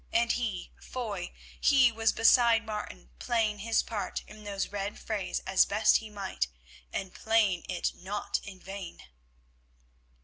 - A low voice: No, high, 210 Hz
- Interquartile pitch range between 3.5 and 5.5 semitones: No, average, 2.7 semitones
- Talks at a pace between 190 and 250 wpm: No, average, 140 wpm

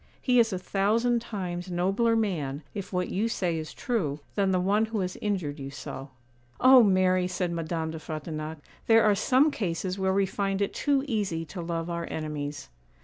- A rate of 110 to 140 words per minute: No, average, 190 wpm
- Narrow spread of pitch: No, average, 4.4 semitones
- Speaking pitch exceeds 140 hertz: Yes, medium, 185 Hz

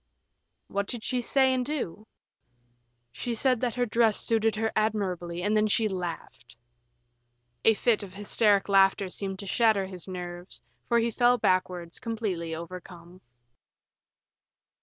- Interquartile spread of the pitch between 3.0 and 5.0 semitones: Yes, average, 3.9 semitones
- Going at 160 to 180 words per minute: No, average, 140 wpm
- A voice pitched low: No, high, 205 Hz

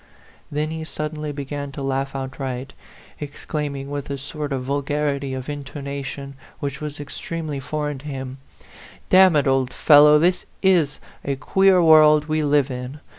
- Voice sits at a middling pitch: Yes, medium, 145 Hz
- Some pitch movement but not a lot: No, narrow, 1.8 semitones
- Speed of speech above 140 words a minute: Yes, average, 155 wpm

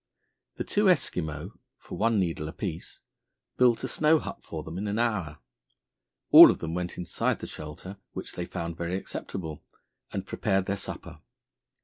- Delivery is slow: No, average, 160 wpm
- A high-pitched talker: No, very low, 90 Hz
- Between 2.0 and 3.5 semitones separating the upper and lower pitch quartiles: No, average, 4.4 semitones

